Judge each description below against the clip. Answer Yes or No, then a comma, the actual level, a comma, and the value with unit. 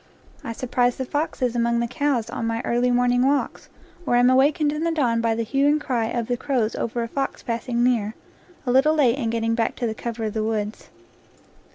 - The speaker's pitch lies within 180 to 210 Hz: No, high, 245 Hz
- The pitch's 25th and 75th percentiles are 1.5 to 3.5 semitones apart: Yes, average, 2.8 semitones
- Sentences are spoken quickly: Yes, fast, 220 wpm